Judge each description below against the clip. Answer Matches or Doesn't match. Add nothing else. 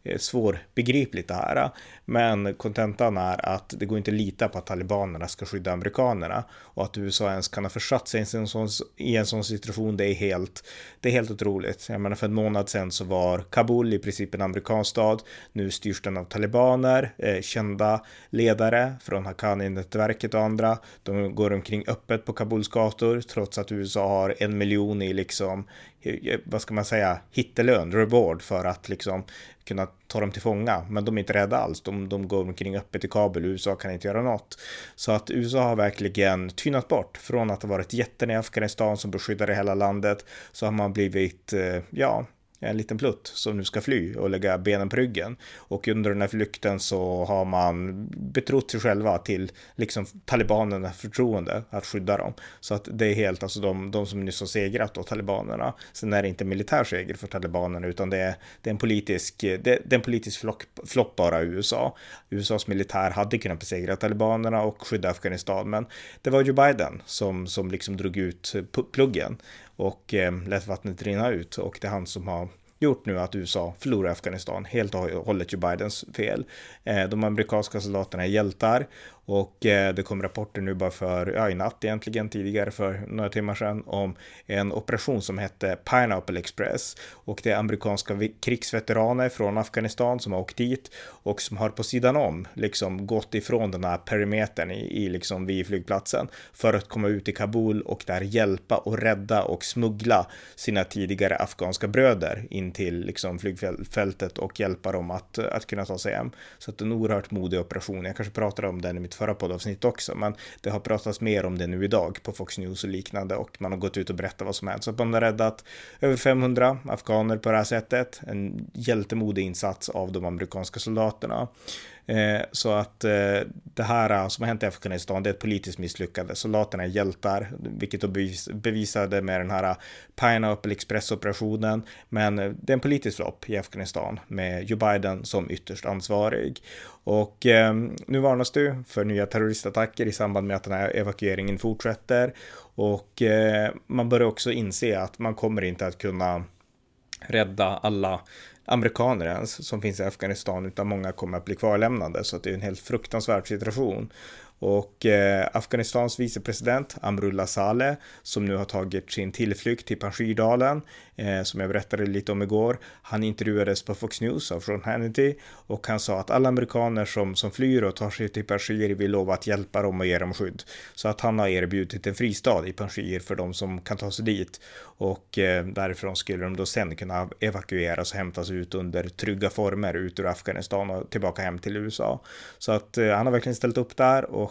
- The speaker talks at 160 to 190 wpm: Matches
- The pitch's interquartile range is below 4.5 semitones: Matches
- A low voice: Matches